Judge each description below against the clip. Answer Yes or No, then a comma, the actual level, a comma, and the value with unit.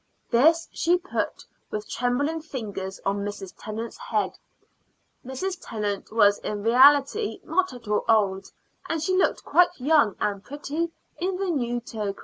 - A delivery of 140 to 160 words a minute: Yes, average, 145 wpm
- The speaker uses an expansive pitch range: Yes, wide, 7.8 semitones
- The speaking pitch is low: No, very high, 250 Hz